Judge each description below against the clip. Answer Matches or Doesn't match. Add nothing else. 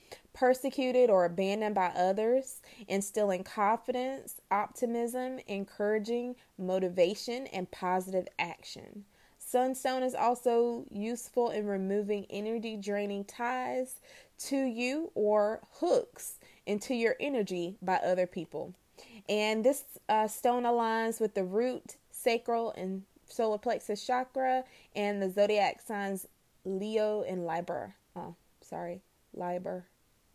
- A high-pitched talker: Matches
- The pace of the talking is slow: Matches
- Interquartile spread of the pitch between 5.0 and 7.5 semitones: Doesn't match